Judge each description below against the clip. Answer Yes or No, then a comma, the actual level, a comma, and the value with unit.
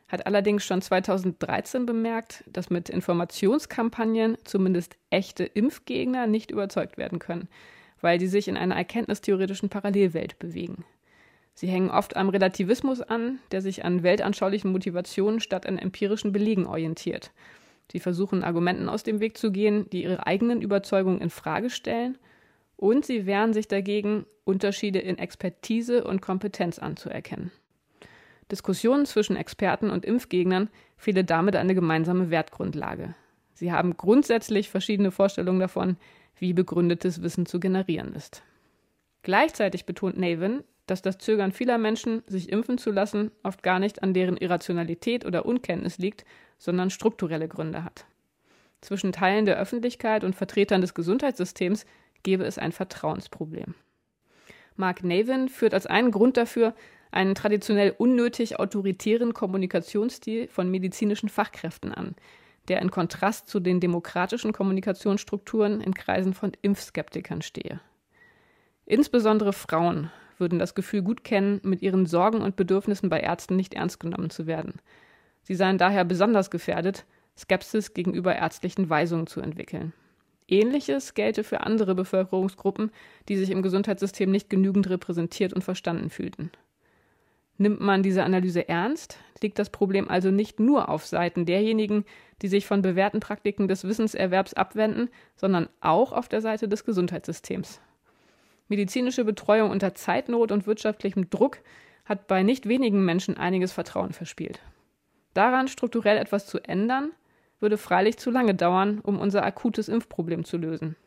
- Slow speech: No, average, 140 wpm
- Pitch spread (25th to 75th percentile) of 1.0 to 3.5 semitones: Yes, average, 2.8 semitones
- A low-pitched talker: No, high, 195 Hz